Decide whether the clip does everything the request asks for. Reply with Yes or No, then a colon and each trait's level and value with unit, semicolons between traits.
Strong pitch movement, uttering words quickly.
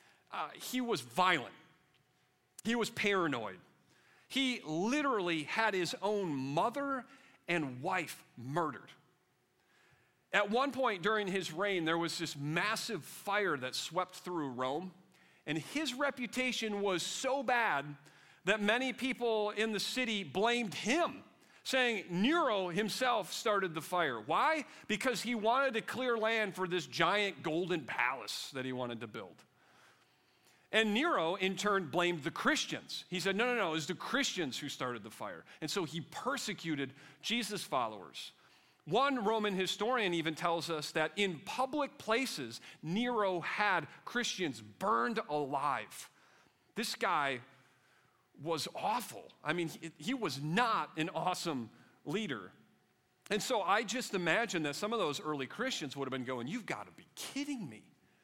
No: wide, 6.7 semitones; average, 145 wpm